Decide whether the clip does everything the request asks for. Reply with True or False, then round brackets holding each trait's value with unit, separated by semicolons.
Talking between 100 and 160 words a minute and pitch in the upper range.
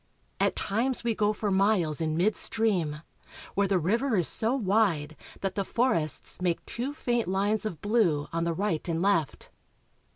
False (170 wpm; 195 Hz)